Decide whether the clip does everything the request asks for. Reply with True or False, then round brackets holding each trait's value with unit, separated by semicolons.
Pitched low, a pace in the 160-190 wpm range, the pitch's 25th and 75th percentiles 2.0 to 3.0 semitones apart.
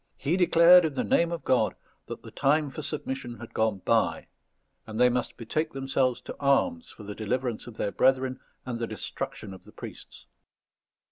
False (130 Hz; 185 wpm; 4.7 semitones)